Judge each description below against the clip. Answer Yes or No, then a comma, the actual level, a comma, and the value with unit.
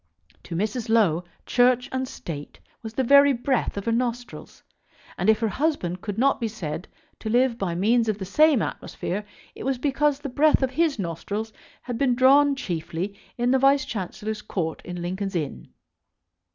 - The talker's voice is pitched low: No, high, 230 Hz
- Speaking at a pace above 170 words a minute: Yes, average, 180 wpm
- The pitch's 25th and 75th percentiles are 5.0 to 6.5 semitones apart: Yes, average, 5.3 semitones